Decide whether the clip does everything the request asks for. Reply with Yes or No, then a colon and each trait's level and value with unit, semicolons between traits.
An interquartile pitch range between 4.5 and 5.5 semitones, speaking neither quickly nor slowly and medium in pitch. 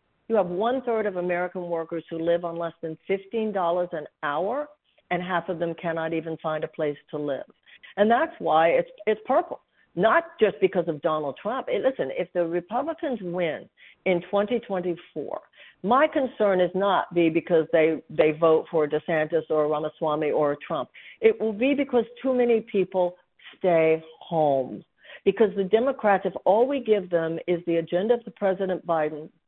Yes: average, 5.1 semitones; average, 175 wpm; medium, 180 Hz